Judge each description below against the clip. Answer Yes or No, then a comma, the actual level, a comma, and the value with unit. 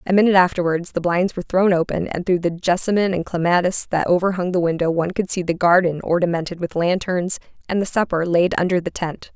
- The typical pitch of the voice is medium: Yes, medium, 175 Hz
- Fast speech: Yes, fast, 210 wpm